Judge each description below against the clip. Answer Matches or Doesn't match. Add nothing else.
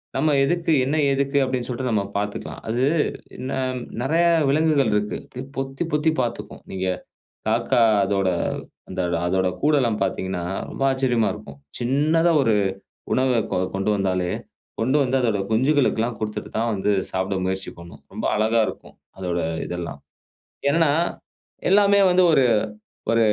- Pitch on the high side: Doesn't match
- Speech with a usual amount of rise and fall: Doesn't match